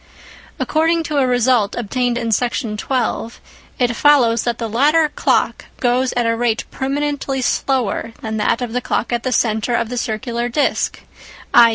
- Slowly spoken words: No, average, 170 wpm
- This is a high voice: Yes, high, 245 Hz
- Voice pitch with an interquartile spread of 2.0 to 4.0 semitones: Yes, narrow, 2.5 semitones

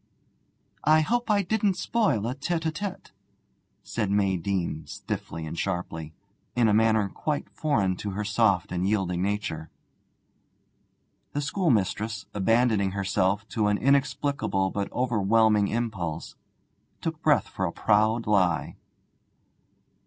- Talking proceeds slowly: Yes, slow, 125 wpm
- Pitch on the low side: Yes, low, 105 Hz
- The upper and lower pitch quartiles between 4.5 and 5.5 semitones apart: Yes, average, 5.1 semitones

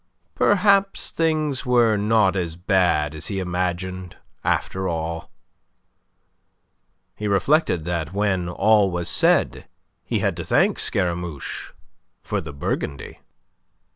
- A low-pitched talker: Yes, very low, 95 Hz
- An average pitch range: Yes, average, 4.1 semitones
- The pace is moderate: No, slow, 110 wpm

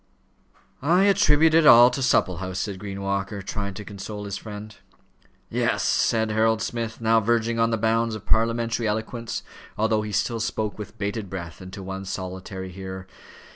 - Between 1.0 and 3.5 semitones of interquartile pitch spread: Yes, average, 2.7 semitones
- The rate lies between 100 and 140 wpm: No, average, 170 wpm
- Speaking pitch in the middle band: No, low, 110 Hz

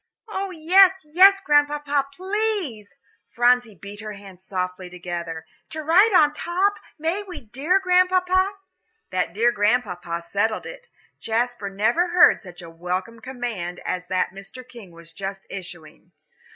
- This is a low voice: No, high, 240 Hz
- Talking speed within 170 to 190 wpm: No, average, 140 wpm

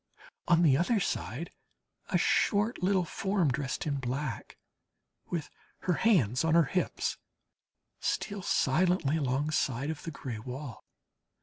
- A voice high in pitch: No, medium, 155 Hz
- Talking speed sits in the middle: No, slow, 125 wpm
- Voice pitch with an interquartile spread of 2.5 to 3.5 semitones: No, average, 5.2 semitones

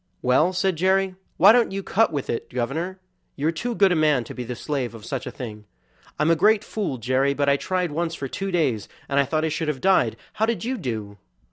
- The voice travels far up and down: Yes, wide, 6.5 semitones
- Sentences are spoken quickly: Yes, fast, 245 wpm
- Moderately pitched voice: Yes, medium, 155 Hz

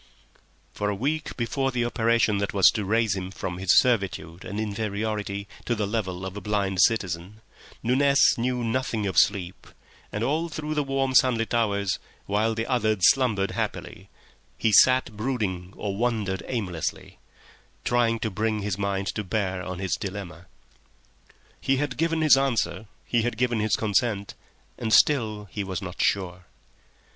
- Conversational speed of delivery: Yes, average, 160 wpm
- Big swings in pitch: No, average, 3.7 semitones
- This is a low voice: Yes, low, 110 Hz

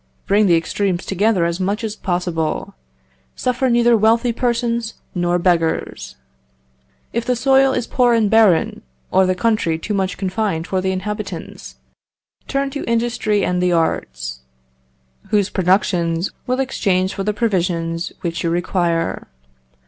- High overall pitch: Yes, high, 195 Hz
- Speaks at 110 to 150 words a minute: Yes, average, 140 wpm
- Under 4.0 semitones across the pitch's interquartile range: No, average, 4.8 semitones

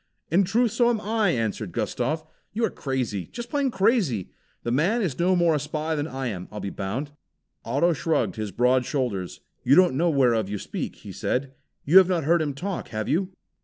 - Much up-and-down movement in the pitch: Yes, wide, 7.4 semitones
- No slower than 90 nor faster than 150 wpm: No, fast, 205 wpm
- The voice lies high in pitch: No, medium, 150 Hz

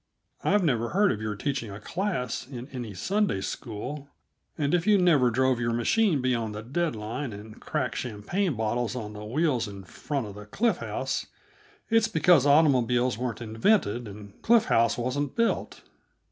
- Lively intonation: Yes, wide, 6.4 semitones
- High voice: No, low, 125 Hz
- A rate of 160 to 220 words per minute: Yes, average, 170 wpm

